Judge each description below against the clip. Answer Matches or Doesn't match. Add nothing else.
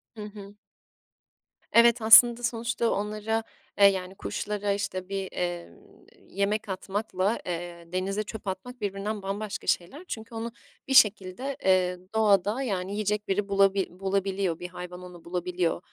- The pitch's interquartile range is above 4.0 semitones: Doesn't match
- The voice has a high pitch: Matches